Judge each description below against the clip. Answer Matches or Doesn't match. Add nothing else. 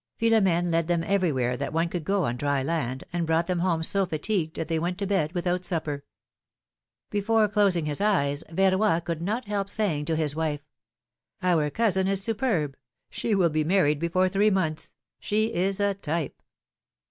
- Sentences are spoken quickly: Doesn't match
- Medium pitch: Matches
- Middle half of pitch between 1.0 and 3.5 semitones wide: Doesn't match